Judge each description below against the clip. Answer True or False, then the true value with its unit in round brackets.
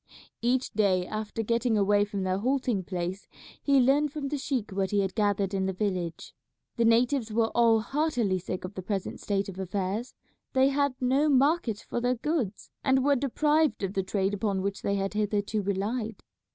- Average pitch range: True (4.8 semitones)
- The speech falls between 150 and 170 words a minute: False (190 wpm)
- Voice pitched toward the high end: True (215 Hz)